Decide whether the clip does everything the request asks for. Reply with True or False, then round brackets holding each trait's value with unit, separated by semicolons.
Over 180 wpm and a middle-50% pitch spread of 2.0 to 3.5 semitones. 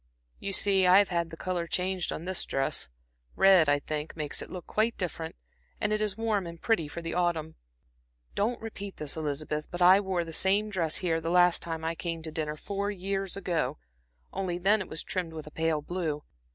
True (205 wpm; 3.2 semitones)